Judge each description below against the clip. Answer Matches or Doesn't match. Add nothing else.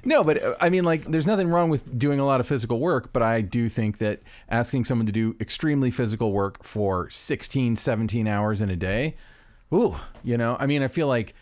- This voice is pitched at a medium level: Doesn't match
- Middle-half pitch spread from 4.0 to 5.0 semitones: Matches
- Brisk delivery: Matches